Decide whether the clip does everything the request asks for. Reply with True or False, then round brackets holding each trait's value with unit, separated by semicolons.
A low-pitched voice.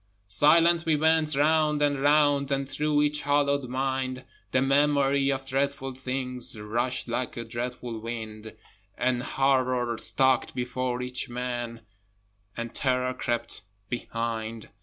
True (130 Hz)